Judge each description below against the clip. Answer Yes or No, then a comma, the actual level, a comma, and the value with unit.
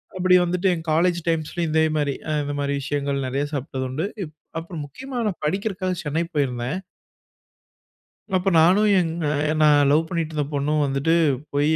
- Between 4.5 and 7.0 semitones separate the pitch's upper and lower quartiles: No, average, 3.5 semitones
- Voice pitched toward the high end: No, medium, 155 Hz